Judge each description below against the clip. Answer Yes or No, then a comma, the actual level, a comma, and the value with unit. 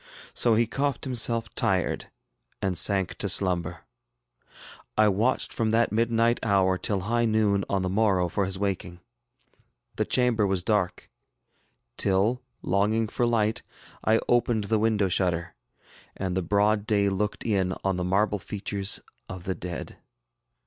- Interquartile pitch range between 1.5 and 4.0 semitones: Yes, average, 2.9 semitones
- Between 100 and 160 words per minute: Yes, average, 145 wpm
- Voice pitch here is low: Yes, low, 100 Hz